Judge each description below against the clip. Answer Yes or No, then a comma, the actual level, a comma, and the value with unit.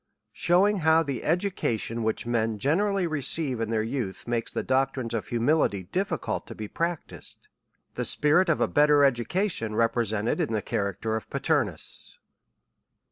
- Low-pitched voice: Yes, low, 130 Hz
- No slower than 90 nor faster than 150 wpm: Yes, average, 145 wpm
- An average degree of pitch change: No, wide, 6.3 semitones